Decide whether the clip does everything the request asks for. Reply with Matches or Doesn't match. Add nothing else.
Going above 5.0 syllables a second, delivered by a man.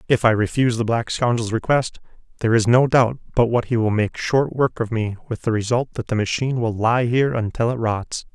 Matches